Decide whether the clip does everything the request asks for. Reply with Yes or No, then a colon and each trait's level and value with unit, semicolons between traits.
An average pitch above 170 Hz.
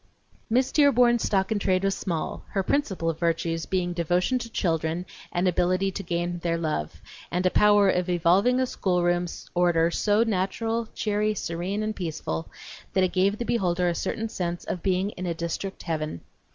Yes: medium, 185 Hz